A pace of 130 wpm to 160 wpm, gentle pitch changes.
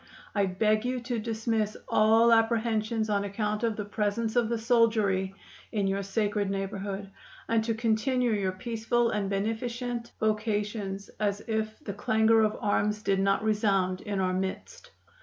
Yes: average, 155 wpm; narrow, 2.2 semitones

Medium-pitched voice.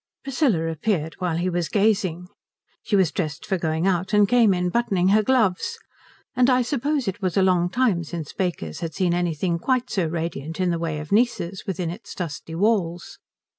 Yes: medium, 180 Hz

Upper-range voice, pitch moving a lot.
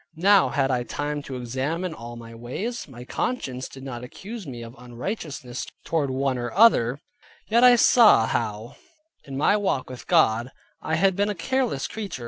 No: low, 135 Hz; wide, 8.2 semitones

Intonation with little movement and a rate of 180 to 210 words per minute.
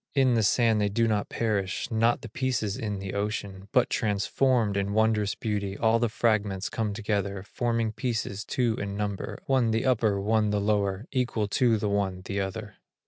Yes: narrow, 2.3 semitones; average, 185 wpm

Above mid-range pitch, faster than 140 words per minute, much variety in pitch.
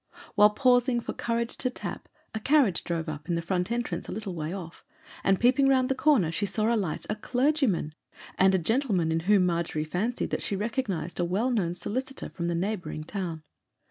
Yes: high, 200 Hz; average, 200 wpm; wide, 6.0 semitones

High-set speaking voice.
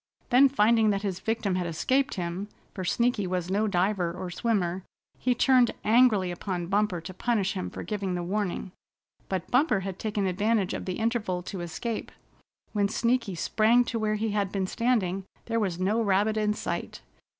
Yes: high, 205 Hz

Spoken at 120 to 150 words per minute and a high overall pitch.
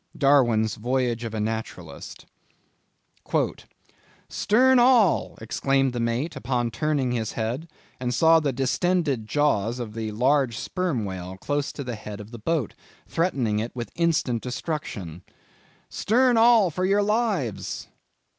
No: slow, 135 wpm; low, 130 Hz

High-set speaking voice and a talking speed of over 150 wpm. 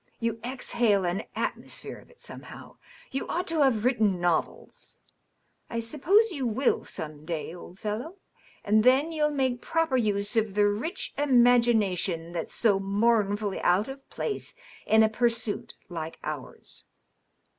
No: high, 220 Hz; average, 145 wpm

